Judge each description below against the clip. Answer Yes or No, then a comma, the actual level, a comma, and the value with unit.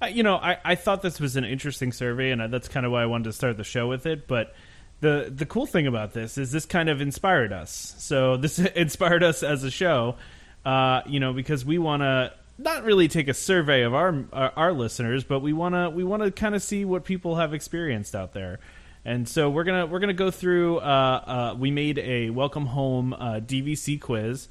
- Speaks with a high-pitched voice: No, medium, 140 Hz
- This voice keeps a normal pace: No, fast, 235 wpm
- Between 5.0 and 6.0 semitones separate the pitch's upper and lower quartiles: Yes, wide, 5.5 semitones